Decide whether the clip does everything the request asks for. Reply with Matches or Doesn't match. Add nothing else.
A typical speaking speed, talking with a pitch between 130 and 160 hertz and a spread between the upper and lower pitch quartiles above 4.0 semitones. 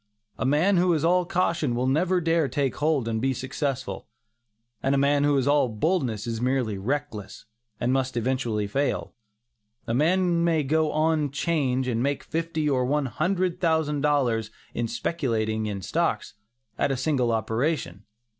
Matches